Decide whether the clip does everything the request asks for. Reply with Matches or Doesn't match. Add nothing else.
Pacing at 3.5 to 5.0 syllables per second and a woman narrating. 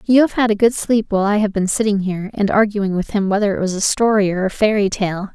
Doesn't match